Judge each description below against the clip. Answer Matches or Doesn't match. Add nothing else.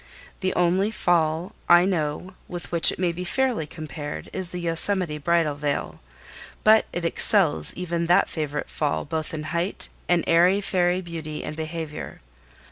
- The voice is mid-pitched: Matches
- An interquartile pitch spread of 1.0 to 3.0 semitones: Matches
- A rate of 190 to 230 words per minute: Doesn't match